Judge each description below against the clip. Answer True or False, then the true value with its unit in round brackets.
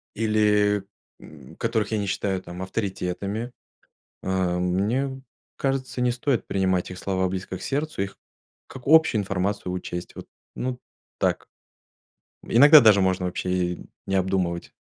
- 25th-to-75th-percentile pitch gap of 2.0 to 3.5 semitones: False (4.2 semitones)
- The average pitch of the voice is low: True (100 Hz)